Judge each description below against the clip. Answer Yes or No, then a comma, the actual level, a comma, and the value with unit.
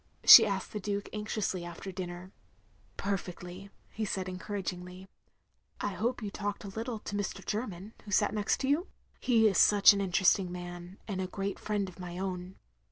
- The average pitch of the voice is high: Yes, high, 195 Hz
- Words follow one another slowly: No, average, 170 wpm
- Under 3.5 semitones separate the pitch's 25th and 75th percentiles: Yes, narrow, 2.4 semitones